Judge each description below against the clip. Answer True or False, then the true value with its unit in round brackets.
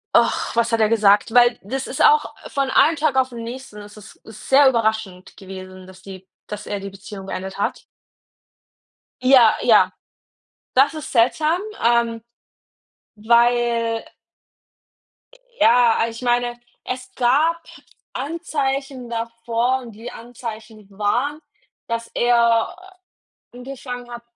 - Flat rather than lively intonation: False (3.1 semitones)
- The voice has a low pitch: False (235 Hz)